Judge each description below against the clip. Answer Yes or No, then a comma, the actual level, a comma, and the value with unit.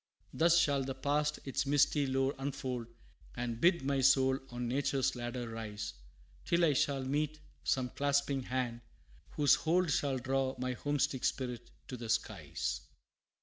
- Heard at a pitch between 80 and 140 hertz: Yes, low, 135 Hz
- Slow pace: No, average, 145 wpm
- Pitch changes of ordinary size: No, narrow, 2.3 semitones